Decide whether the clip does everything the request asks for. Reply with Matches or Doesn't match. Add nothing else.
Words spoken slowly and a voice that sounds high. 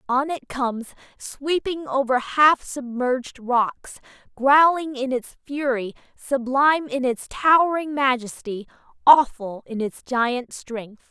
Matches